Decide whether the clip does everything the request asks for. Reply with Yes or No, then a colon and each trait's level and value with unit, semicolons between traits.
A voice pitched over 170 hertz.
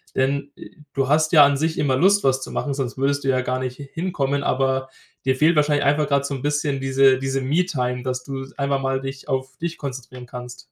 No: low, 135 Hz